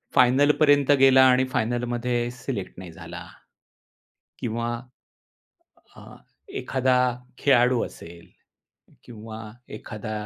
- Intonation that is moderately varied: Yes, average, 3.1 semitones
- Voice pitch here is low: Yes, low, 120 Hz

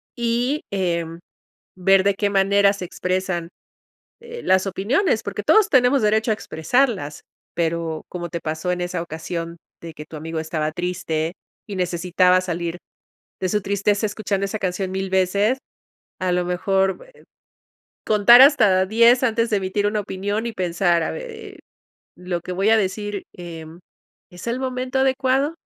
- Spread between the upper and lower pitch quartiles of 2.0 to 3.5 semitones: No, average, 3.9 semitones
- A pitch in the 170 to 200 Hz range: Yes, high, 190 Hz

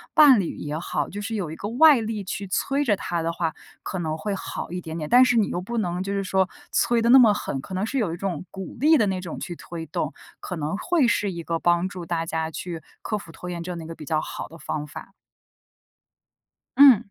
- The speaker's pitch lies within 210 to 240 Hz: No, medium, 185 Hz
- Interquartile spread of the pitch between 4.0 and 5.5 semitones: Yes, average, 4.7 semitones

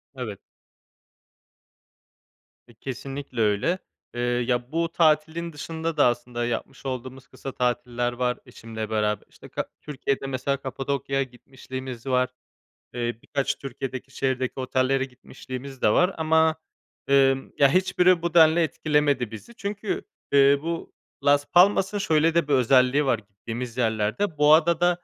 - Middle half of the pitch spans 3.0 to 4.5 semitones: Yes, average, 4.2 semitones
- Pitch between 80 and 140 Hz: Yes, low, 135 Hz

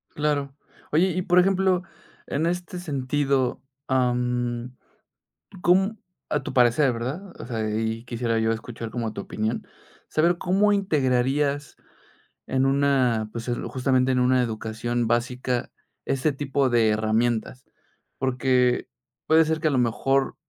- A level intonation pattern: No, average, 3.8 semitones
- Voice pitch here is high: No, low, 130 Hz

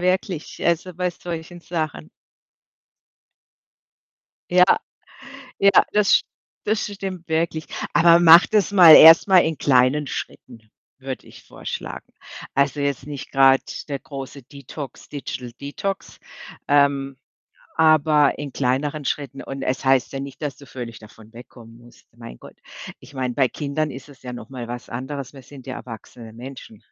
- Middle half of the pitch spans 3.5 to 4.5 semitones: Yes, average, 3.9 semitones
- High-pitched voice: No, medium, 140 Hz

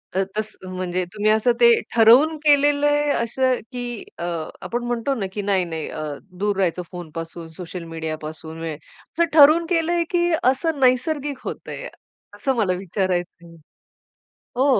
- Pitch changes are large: Yes, wide, 8.1 semitones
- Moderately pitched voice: No, high, 225 Hz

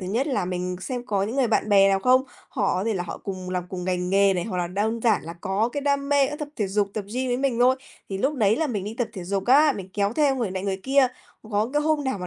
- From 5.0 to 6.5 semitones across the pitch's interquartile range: Yes, wide, 5.4 semitones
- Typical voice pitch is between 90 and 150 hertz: No, high, 210 Hz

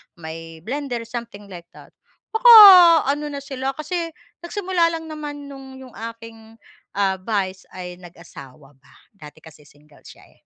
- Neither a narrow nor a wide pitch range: No, wide, 8.8 semitones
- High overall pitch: Yes, high, 225 Hz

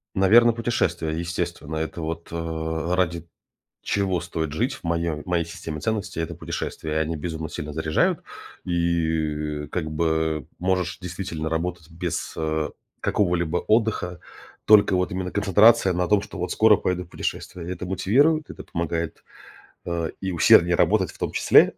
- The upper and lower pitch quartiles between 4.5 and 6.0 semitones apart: No, average, 2.7 semitones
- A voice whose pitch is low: Yes, very low, 85 Hz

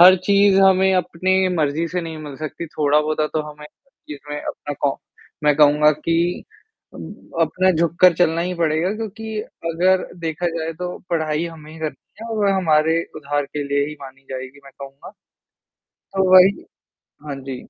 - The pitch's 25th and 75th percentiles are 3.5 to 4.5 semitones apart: Yes, average, 3.8 semitones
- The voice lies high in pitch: No, medium, 160 Hz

